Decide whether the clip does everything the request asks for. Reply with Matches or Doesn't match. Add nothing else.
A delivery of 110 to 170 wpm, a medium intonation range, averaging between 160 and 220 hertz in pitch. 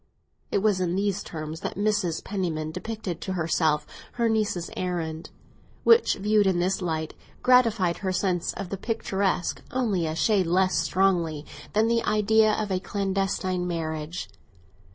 Matches